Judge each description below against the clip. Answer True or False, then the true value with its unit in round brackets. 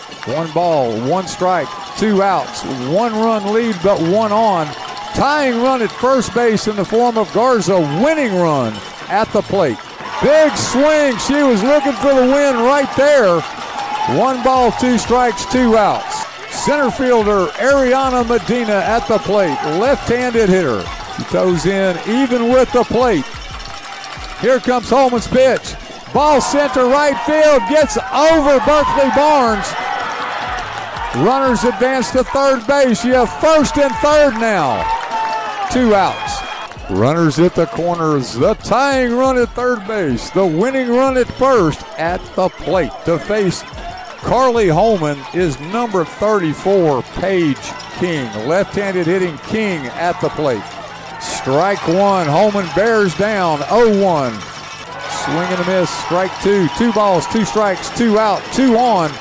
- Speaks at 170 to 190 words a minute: False (140 wpm)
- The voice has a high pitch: True (225 Hz)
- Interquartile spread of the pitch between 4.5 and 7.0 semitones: True (5.6 semitones)